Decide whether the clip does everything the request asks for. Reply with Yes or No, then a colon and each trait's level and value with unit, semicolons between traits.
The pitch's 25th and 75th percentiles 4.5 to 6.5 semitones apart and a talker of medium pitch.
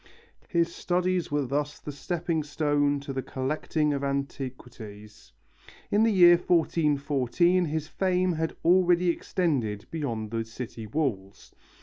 Yes: average, 4.8 semitones; medium, 145 Hz